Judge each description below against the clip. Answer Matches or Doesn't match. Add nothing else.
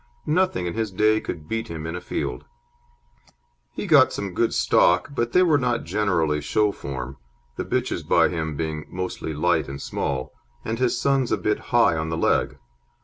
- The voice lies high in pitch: Doesn't match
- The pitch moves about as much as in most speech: Doesn't match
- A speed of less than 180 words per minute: Doesn't match